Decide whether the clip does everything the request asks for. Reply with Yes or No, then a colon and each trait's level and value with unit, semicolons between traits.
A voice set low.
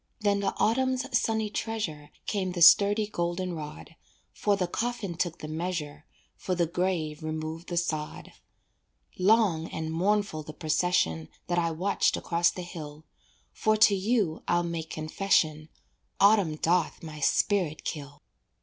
No: medium, 175 Hz